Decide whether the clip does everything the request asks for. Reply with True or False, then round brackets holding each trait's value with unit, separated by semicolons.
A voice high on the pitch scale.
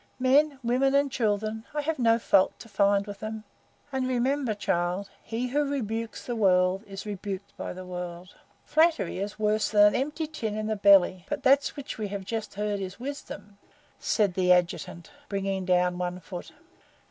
True (210 Hz)